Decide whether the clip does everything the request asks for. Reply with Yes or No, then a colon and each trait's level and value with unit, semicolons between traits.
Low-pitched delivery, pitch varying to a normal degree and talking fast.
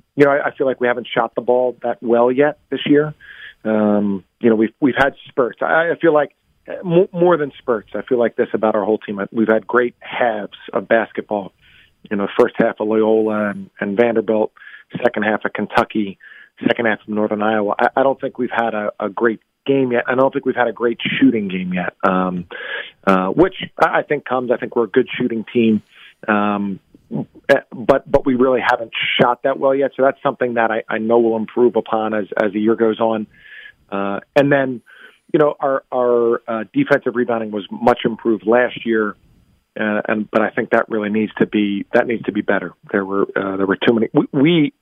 Yes: low, 115 Hz; average, 3.2 semitones; fast, 215 wpm